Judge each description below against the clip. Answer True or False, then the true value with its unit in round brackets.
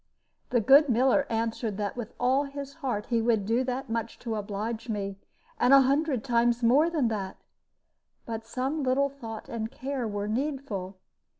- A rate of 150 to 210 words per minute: True (170 wpm)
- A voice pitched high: True (240 Hz)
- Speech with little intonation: False (3.6 semitones)